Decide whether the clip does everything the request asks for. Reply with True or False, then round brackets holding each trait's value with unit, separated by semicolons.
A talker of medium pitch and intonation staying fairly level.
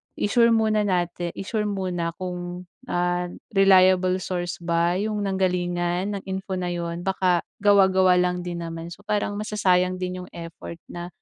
True (180 Hz; 1.8 semitones)